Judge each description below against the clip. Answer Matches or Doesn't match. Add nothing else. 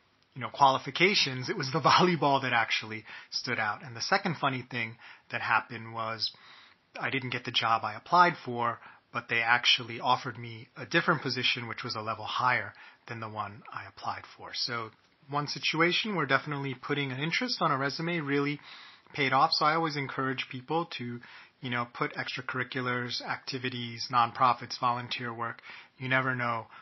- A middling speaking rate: Matches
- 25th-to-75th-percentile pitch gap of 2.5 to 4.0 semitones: Matches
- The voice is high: Doesn't match